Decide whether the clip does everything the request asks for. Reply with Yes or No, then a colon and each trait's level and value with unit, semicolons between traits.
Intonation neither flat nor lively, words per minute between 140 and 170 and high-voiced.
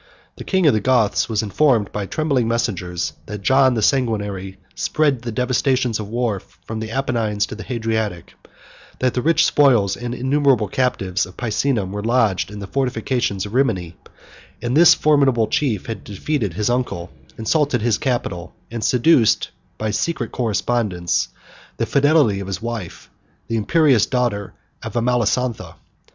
No: average, 4.0 semitones; average, 155 wpm; low, 115 Hz